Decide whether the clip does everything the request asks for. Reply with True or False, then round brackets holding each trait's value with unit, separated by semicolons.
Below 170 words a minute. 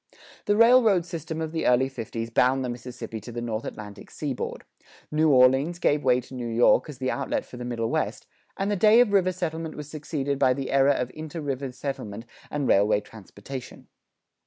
False (195 wpm)